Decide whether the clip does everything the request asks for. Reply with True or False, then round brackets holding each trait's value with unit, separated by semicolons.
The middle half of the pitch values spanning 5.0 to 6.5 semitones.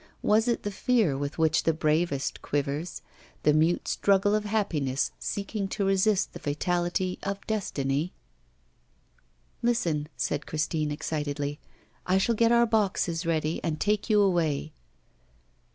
True (5.3 semitones)